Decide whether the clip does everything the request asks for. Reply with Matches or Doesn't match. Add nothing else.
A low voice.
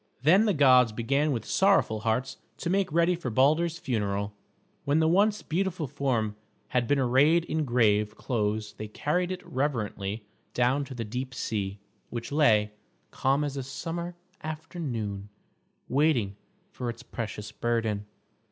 Matches